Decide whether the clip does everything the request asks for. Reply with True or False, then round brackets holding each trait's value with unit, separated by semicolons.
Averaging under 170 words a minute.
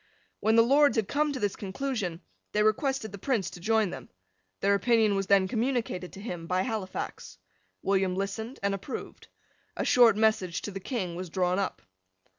False (180 wpm)